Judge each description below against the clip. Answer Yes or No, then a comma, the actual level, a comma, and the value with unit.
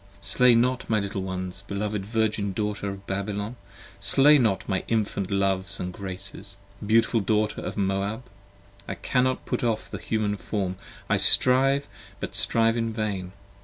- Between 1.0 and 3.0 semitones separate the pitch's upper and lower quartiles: Yes, narrow, 2.6 semitones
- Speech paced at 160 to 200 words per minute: No, average, 150 wpm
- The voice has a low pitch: Yes, low, 105 Hz